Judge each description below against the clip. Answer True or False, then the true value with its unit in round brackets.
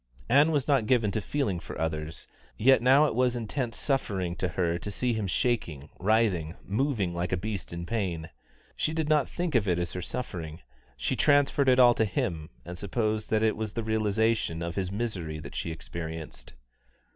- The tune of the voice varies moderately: False (6.2 semitones)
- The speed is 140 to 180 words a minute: False (190 wpm)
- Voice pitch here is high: False (105 Hz)